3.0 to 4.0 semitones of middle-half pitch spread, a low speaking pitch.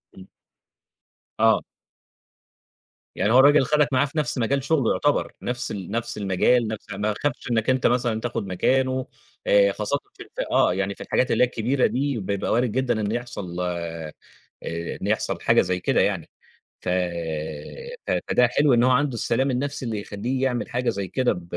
No: average, 4.4 semitones; low, 120 Hz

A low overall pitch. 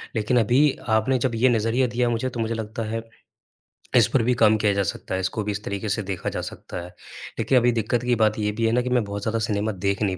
Yes: low, 110 Hz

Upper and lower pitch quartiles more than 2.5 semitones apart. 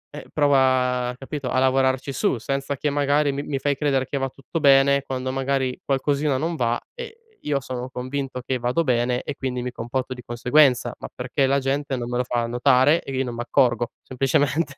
No: narrow, 2.0 semitones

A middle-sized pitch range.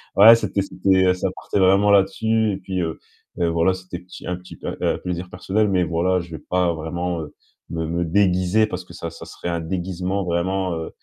No: narrow, 1.9 semitones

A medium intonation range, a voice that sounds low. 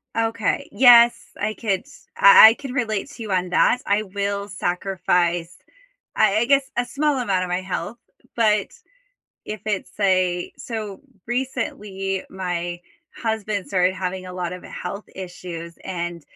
No: average, 3.7 semitones; high, 200 Hz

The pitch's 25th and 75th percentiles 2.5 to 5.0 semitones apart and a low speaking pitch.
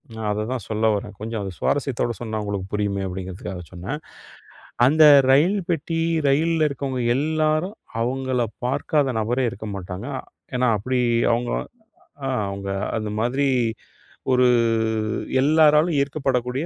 No: wide, 5.4 semitones; low, 125 Hz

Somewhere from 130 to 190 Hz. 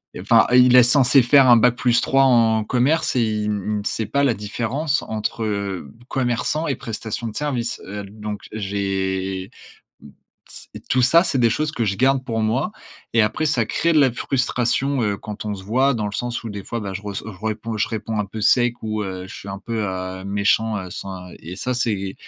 No: low, 110 Hz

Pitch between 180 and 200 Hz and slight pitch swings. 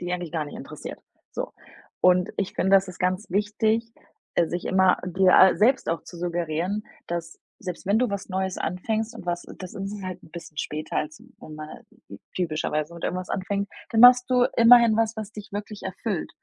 No: high, 190 Hz; average, 3.4 semitones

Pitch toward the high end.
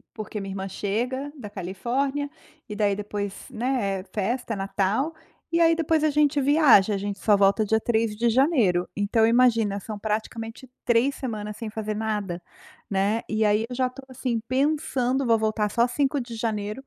Yes: high, 225 Hz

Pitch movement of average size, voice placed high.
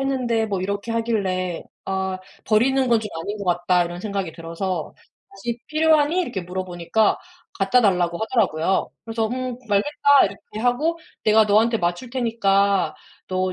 Yes: average, 4.5 semitones; high, 210 Hz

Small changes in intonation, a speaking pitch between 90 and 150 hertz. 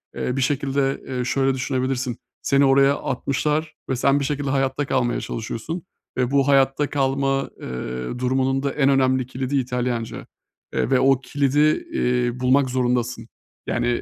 Yes: narrow, 1.6 semitones; low, 135 Hz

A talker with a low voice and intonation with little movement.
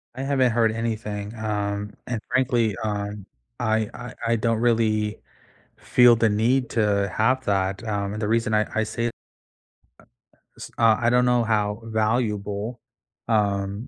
Yes: low, 110 Hz; narrow, 2.1 semitones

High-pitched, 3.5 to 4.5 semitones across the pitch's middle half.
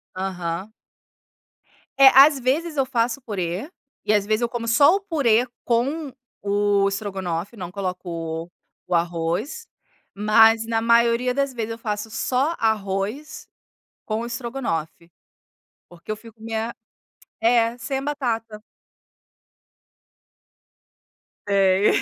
Yes: high, 225 Hz; average, 4.1 semitones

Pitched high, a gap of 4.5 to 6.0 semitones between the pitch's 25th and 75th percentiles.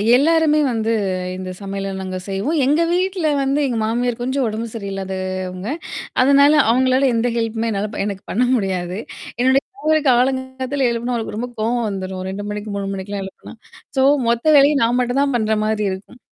Yes: high, 235 Hz; average, 4.9 semitones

